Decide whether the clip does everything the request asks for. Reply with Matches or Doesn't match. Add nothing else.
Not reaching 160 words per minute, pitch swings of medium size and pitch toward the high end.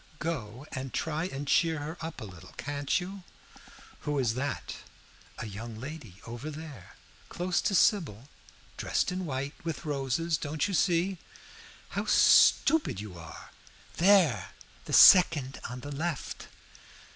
Doesn't match